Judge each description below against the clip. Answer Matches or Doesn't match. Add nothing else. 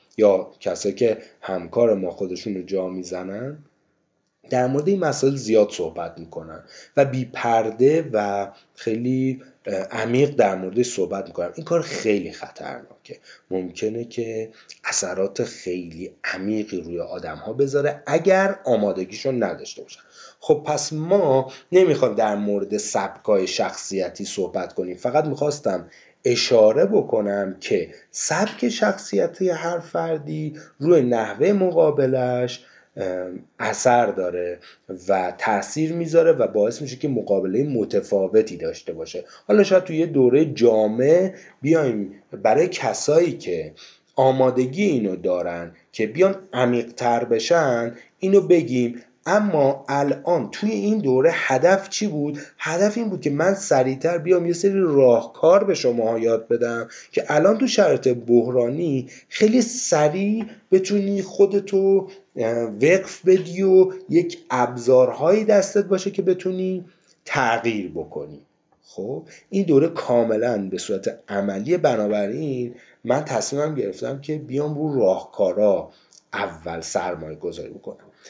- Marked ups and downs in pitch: Matches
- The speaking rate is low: Doesn't match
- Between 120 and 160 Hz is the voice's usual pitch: Matches